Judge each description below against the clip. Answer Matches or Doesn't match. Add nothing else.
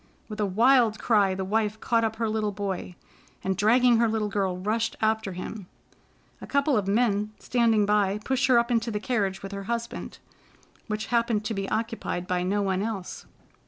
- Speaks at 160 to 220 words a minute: Matches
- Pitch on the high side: Matches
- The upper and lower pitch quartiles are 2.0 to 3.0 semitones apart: Matches